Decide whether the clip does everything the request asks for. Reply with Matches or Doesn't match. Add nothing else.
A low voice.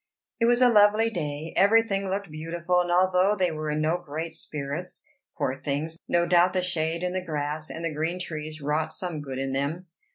Doesn't match